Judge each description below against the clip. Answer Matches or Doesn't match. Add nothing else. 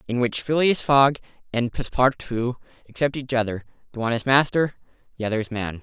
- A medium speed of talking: Matches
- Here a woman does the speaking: Doesn't match